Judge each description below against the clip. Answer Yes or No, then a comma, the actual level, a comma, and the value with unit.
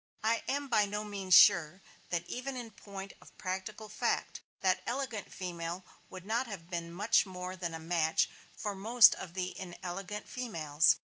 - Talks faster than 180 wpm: No, average, 165 wpm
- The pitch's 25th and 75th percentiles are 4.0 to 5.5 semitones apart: No, average, 3.5 semitones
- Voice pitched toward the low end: No, high, 190 Hz